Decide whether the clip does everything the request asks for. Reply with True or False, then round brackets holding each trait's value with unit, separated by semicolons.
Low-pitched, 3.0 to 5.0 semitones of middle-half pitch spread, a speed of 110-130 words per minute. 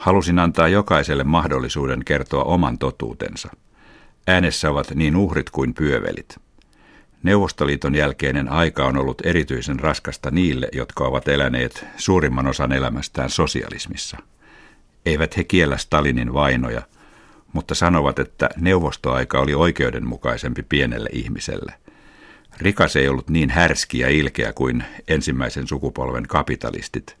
True (70 Hz; 4.1 semitones; 115 wpm)